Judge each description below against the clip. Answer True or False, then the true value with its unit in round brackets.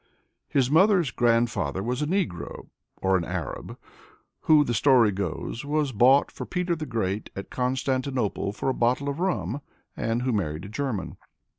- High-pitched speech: False (125 Hz)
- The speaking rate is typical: True (170 wpm)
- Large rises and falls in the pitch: True (5.8 semitones)